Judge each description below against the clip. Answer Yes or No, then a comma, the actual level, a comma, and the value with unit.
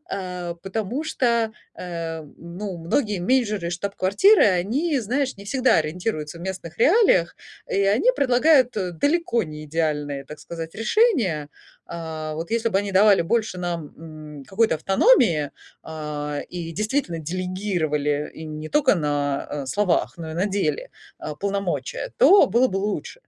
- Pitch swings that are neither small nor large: No, wide, 6.1 semitones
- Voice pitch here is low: No, medium, 185 Hz